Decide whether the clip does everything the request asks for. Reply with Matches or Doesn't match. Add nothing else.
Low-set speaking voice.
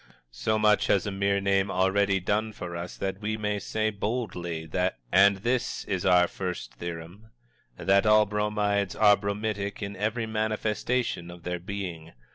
Matches